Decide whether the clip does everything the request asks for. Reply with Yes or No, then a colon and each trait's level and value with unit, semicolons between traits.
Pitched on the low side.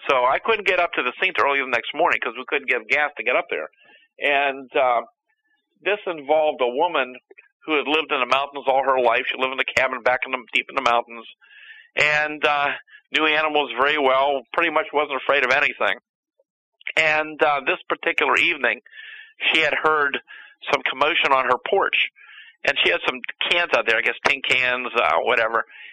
No: medium, 150 Hz